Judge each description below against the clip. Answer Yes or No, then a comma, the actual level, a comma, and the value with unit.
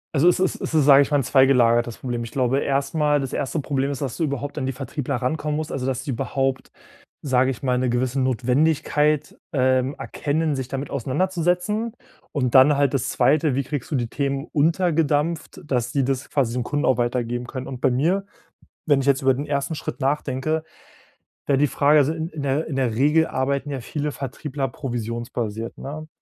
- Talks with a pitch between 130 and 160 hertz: Yes, medium, 140 Hz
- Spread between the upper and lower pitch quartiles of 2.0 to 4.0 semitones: Yes, narrow, 2.6 semitones